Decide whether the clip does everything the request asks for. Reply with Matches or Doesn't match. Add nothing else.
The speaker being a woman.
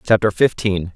Doesn't match